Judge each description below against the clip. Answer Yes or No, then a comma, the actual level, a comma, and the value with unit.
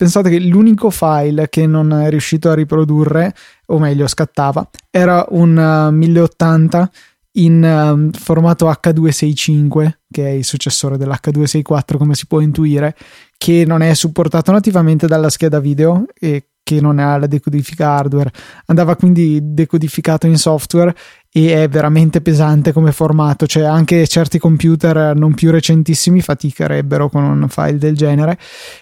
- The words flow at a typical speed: Yes, average, 140 wpm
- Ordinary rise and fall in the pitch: No, narrow, 1.8 semitones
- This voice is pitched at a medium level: Yes, medium, 155 Hz